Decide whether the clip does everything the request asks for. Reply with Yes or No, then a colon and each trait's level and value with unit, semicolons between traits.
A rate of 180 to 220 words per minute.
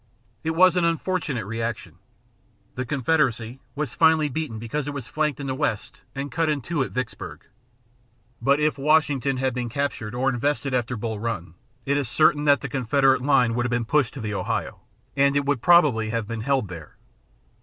Yes: average, 190 wpm